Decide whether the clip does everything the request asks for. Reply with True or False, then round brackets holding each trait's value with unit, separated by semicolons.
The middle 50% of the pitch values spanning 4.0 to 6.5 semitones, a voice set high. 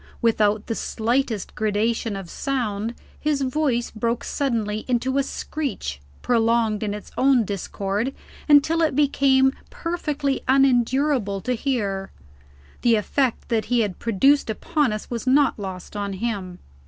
True (4.5 semitones; 235 Hz)